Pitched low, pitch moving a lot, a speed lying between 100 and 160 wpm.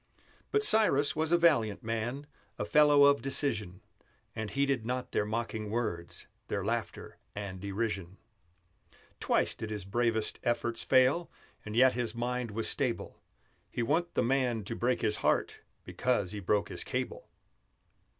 No: low, 120 Hz; average, 4.3 semitones; average, 150 wpm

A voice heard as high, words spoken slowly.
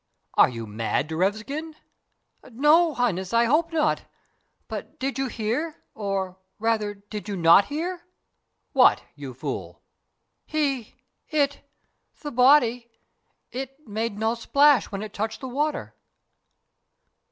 Yes: high, 235 Hz; slow, 120 wpm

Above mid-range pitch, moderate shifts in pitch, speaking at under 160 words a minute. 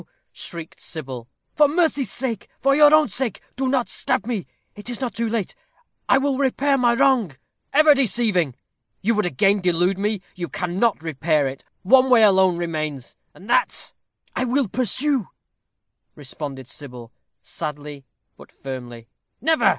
No: high, 205 Hz; wide, 8.7 semitones; average, 150 wpm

